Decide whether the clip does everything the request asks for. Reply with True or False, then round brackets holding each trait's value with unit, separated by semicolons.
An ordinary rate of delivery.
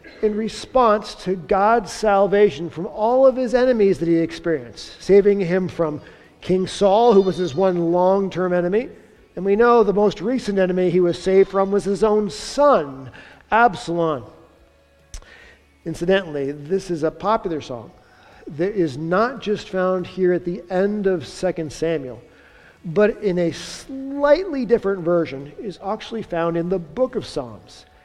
True (155 wpm)